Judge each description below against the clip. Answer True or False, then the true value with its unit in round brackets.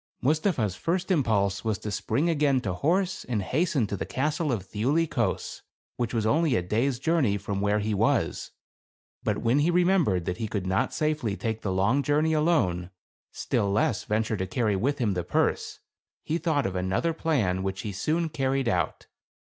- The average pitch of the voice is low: True (115 Hz)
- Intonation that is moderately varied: False (7.4 semitones)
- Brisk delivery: False (195 wpm)